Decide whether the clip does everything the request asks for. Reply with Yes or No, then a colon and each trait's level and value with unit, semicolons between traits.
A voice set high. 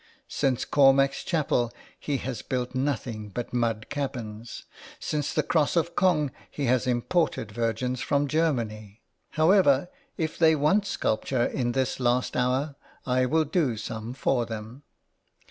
No: low, 130 Hz